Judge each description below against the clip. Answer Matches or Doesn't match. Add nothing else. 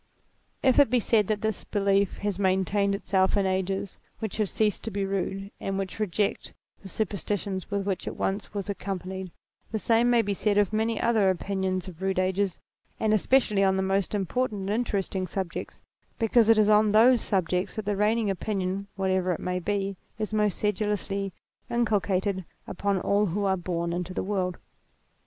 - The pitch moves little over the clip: Matches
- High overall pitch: Matches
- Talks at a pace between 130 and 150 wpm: Doesn't match